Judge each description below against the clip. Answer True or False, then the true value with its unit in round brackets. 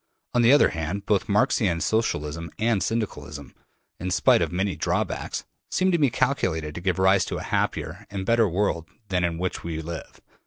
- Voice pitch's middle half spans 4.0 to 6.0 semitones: True (4.6 semitones)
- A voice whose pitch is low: True (95 Hz)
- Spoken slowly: False (190 wpm)